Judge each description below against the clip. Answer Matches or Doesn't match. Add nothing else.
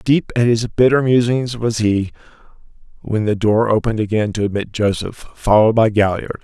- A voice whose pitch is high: Doesn't match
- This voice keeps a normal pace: Matches